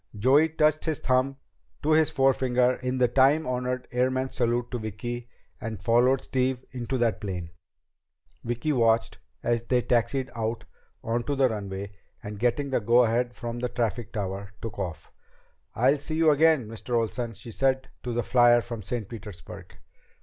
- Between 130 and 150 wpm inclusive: No, average, 165 wpm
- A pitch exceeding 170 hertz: No, low, 120 Hz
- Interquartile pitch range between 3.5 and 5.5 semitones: No, narrow, 2.4 semitones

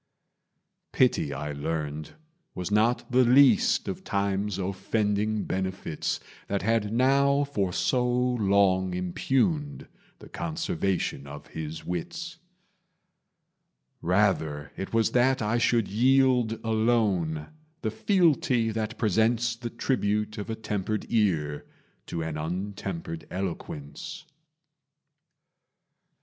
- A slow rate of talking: Yes, slow, 105 wpm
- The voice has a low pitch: Yes, low, 105 Hz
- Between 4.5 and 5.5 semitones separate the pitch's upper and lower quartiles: Yes, average, 5.2 semitones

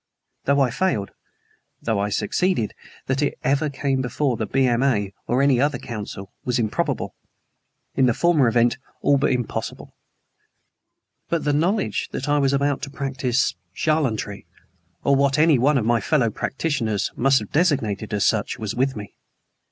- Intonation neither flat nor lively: Yes, average, 4.1 semitones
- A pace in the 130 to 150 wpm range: No, average, 160 wpm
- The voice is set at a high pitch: No, low, 130 Hz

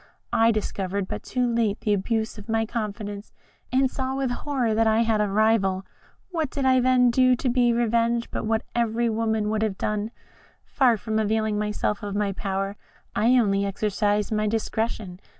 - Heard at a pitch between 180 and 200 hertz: No, high, 220 Hz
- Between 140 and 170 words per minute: No, average, 180 wpm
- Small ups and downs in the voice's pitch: Yes, narrow, 2.3 semitones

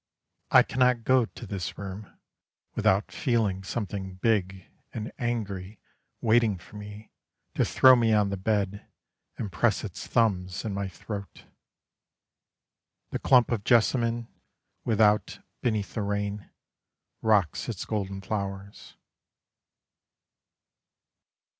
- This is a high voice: No, low, 105 Hz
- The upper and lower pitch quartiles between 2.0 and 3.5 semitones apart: Yes, average, 2.7 semitones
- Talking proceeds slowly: Yes, slow, 110 wpm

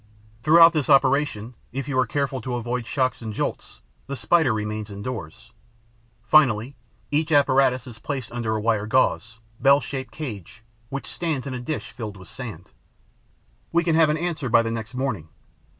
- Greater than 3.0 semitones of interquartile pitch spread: Yes, average, 4.1 semitones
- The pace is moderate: Yes, average, 170 wpm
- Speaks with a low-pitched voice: Yes, low, 130 Hz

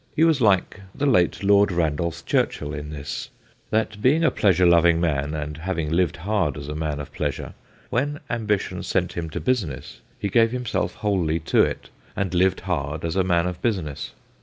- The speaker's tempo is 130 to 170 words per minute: No, average, 185 wpm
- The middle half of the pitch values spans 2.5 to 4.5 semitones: No, average, 5.1 semitones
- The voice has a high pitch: No, very low, 90 Hz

